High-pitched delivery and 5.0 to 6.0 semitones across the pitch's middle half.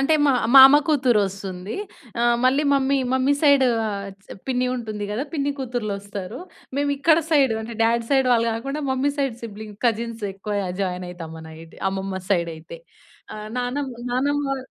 Yes: high, 235 Hz; wide, 5.4 semitones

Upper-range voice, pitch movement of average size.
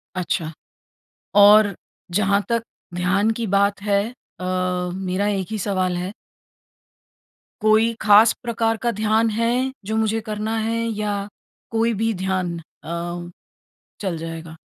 Yes: high, 205 Hz; average, 3.2 semitones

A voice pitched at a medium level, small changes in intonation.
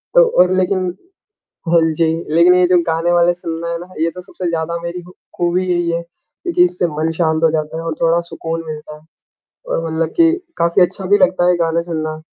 Yes: medium, 170 Hz; narrow, 1.6 semitones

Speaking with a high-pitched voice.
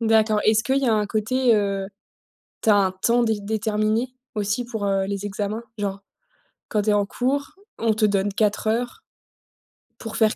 Yes: high, 215 Hz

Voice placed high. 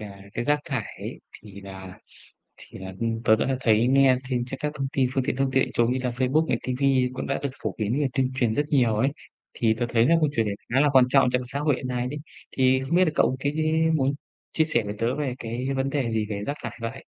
No: low, 130 Hz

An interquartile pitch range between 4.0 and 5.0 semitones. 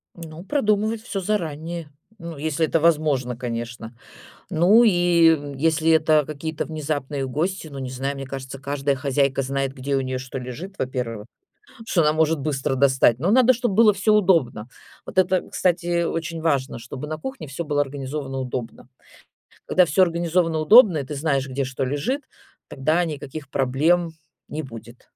Yes: average, 4.3 semitones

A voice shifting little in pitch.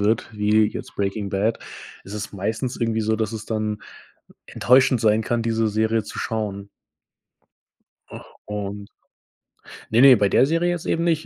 Yes: narrow, 1.8 semitones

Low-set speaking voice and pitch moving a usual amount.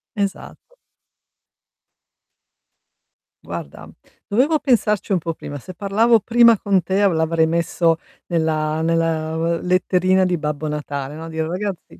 No: medium, 170 Hz; average, 3.8 semitones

